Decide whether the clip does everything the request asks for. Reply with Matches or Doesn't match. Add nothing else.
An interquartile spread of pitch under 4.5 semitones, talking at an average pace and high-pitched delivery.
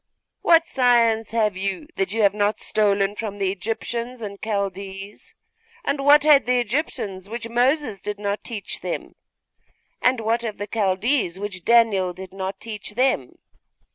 Matches